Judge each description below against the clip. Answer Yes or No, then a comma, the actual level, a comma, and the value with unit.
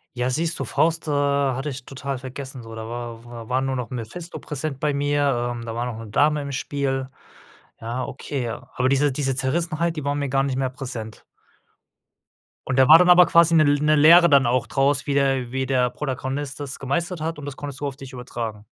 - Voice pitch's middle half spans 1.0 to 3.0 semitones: Yes, narrow, 2.6 semitones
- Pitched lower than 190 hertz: Yes, low, 135 Hz